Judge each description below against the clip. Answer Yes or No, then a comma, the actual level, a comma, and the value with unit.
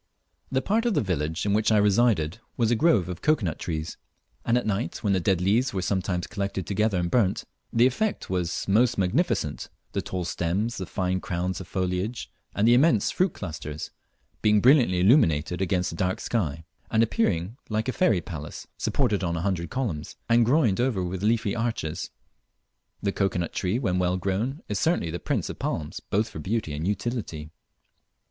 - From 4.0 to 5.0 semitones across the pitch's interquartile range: Yes, average, 4.6 semitones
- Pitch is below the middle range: Yes, low, 100 Hz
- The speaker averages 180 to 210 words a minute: Yes, average, 190 wpm